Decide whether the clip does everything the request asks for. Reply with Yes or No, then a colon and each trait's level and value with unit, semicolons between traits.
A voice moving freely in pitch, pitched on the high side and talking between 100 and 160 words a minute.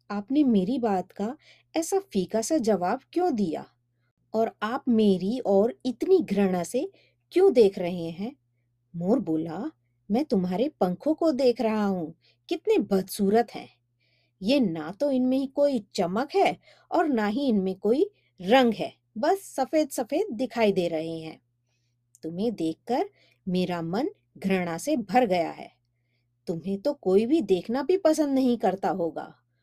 Yes: wide, 7.9 semitones; high, 215 Hz; average, 150 wpm